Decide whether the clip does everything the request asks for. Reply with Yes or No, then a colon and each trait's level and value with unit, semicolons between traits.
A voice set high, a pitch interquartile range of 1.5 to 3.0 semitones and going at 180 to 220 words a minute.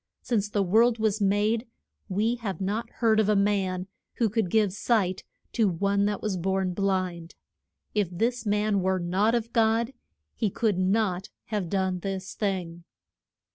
No: high, 200 Hz; average, 2.7 semitones; average, 160 wpm